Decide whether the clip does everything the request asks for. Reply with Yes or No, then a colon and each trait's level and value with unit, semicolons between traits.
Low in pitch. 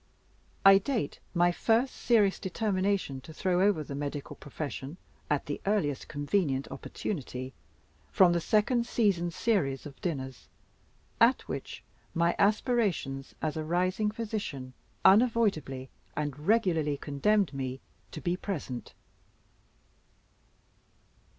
No: medium, 175 Hz